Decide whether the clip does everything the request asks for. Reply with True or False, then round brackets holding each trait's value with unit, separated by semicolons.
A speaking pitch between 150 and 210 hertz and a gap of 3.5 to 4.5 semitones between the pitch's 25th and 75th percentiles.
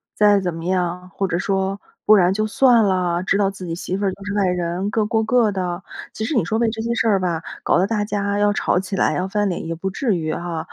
False (195 Hz; 2.7 semitones)